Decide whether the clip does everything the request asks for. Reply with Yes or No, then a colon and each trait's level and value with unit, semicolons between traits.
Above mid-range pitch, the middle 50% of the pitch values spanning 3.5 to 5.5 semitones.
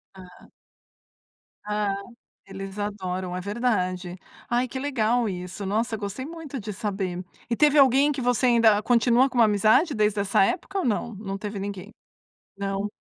Yes: high, 210 Hz; average, 3.9 semitones